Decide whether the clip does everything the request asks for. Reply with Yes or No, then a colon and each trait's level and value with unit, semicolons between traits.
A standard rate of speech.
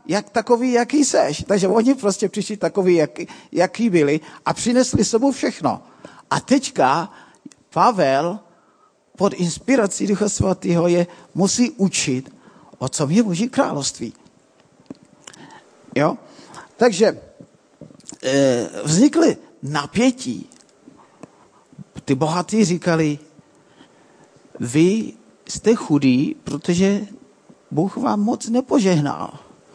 No: slow, 95 wpm